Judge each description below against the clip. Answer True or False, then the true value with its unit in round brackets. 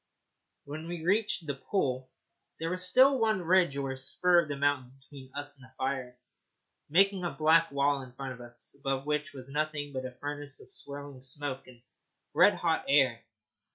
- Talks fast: False (185 wpm)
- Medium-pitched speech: True (145 Hz)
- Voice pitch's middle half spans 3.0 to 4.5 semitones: True (3.5 semitones)